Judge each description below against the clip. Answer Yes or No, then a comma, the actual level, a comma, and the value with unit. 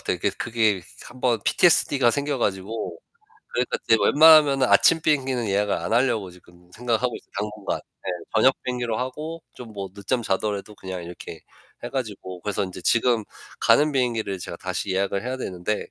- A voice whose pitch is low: Yes, low, 115 Hz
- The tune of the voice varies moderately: Yes, average, 4.6 semitones